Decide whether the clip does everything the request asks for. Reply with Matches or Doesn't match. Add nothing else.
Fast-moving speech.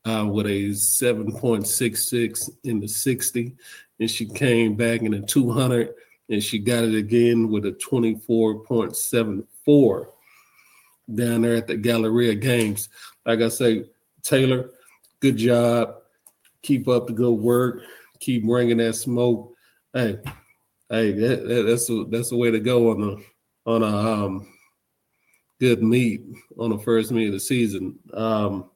Doesn't match